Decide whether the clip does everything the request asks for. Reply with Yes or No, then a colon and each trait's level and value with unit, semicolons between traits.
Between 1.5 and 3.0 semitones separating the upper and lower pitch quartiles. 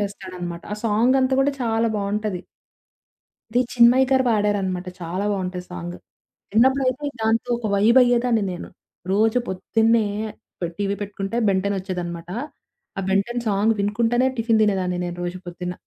No: average, 3.9 semitones